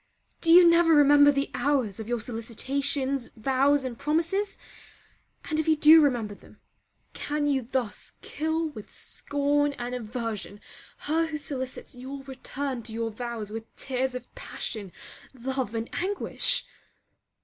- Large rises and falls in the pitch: No, average, 3.8 semitones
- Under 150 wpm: Yes, average, 140 wpm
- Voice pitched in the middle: No, very high, 270 Hz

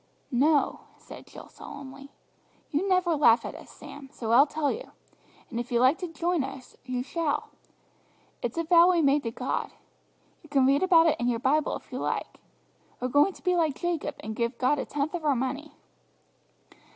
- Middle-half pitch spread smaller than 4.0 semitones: No, average, 4.3 semitones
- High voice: Yes, very high, 285 Hz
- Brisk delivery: No, average, 195 wpm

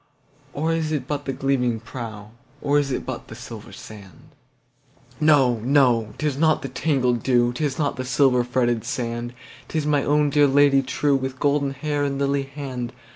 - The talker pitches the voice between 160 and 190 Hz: No, low, 135 Hz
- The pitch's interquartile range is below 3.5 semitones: Yes, average, 2.9 semitones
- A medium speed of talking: Yes, average, 160 wpm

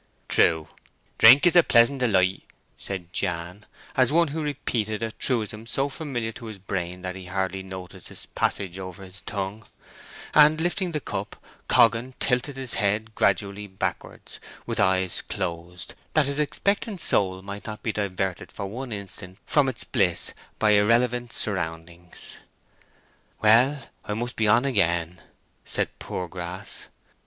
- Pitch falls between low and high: No, low, 105 Hz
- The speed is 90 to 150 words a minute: Yes, average, 145 wpm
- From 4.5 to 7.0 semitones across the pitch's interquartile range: Yes, average, 5.1 semitones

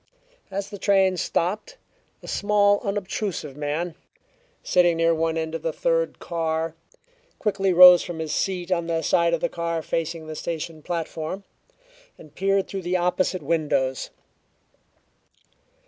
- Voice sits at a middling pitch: Yes, medium, 170 Hz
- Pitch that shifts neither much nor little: Yes, average, 3.0 semitones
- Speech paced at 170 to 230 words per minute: No, average, 140 wpm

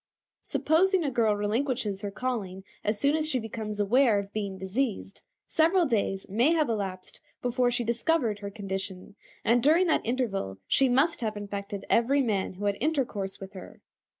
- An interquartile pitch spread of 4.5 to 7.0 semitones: Yes, average, 5.0 semitones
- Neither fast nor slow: Yes, average, 170 wpm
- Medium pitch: No, high, 225 Hz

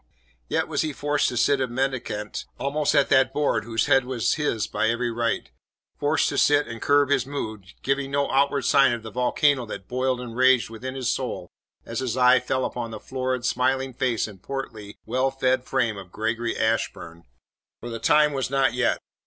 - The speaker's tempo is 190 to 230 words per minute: Yes, average, 195 wpm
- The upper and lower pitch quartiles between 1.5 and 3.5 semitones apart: Yes, average, 2.8 semitones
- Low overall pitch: Yes, low, 130 Hz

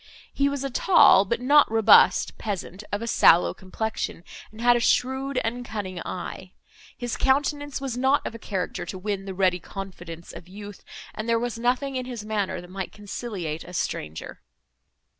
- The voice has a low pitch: No, high, 220 Hz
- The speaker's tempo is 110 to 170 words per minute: No, average, 180 wpm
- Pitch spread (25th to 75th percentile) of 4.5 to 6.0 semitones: Yes, average, 5.0 semitones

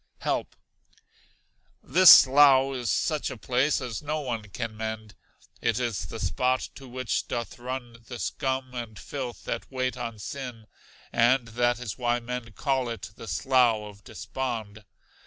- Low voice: Yes, low, 120 Hz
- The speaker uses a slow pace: No, average, 155 wpm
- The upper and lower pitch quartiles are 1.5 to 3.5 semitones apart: Yes, narrow, 2.5 semitones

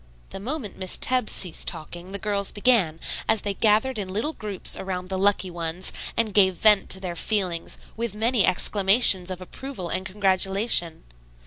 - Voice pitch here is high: Yes, high, 195 Hz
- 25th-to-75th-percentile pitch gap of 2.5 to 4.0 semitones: Yes, average, 2.8 semitones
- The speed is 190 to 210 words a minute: No, average, 165 wpm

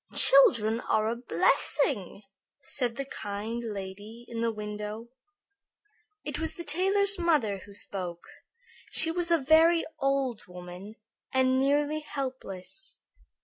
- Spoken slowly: Yes, slow, 120 wpm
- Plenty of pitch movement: Yes, wide, 6.7 semitones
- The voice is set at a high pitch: Yes, high, 240 Hz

